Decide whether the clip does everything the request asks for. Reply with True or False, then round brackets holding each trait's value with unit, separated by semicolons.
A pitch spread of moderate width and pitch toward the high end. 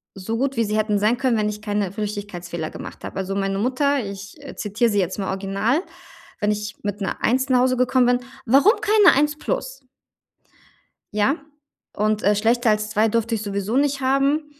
True (4.1 semitones; 215 Hz)